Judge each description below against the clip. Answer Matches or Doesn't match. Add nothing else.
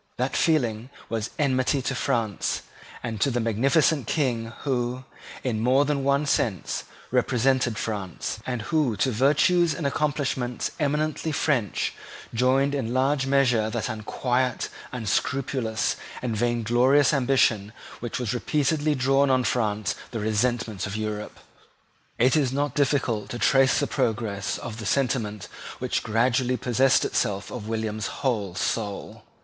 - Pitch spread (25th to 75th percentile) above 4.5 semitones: Doesn't match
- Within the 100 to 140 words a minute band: Matches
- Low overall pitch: Matches